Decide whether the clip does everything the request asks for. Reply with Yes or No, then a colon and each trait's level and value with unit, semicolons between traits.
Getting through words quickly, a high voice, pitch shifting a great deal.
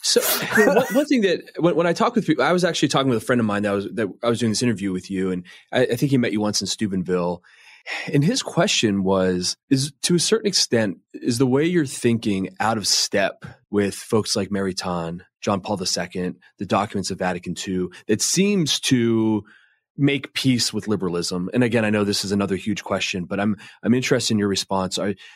No: fast, 220 wpm; low, 105 Hz; wide, 6.2 semitones